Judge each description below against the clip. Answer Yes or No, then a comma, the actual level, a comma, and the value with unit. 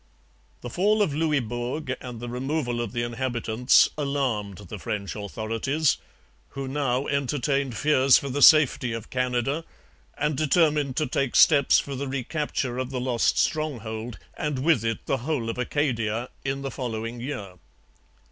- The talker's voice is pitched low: Yes, low, 130 Hz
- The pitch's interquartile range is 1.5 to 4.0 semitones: Yes, average, 3.4 semitones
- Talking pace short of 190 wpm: Yes, average, 150 wpm